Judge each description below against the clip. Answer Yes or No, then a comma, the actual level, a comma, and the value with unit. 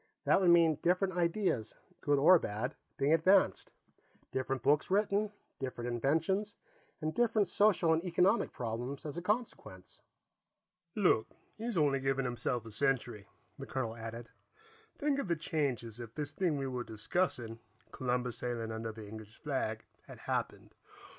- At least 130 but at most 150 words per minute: Yes, average, 145 wpm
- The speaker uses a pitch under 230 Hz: Yes, medium, 140 Hz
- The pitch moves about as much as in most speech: No, wide, 7.1 semitones